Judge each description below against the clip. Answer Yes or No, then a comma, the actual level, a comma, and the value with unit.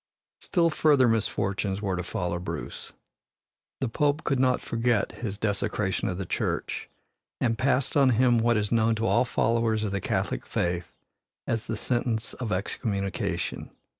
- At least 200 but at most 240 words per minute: No, average, 155 wpm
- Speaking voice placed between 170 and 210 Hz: No, low, 115 Hz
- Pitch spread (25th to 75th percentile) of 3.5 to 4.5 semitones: Yes, average, 3.9 semitones